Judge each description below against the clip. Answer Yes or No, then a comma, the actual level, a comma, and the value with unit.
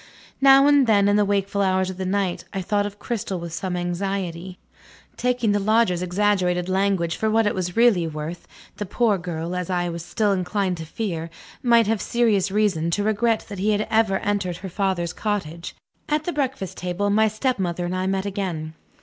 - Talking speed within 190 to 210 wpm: Yes, average, 195 wpm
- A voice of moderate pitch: No, high, 195 Hz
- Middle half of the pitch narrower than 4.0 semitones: Yes, average, 3.2 semitones